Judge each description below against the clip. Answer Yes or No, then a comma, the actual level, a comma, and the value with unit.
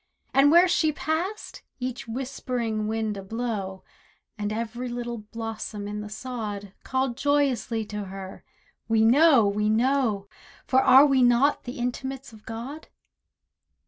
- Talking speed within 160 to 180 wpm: No, slow, 135 wpm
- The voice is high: Yes, high, 235 Hz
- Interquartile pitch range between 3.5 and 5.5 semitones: Yes, average, 3.8 semitones